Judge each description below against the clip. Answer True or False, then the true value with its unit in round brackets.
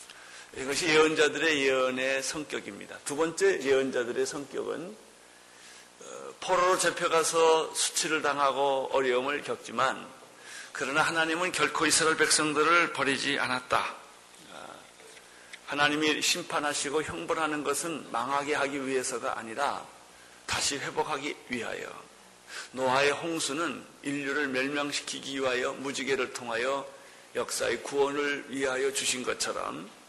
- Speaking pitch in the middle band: True (145 Hz)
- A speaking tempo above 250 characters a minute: True (285 characters per minute)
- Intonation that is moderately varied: True (3.2 semitones)